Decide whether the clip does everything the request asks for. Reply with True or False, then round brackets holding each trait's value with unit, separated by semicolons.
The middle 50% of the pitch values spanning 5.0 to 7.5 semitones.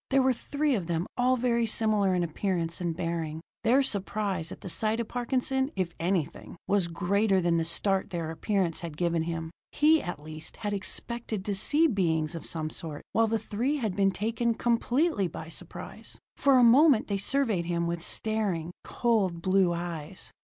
True (5.4 semitones)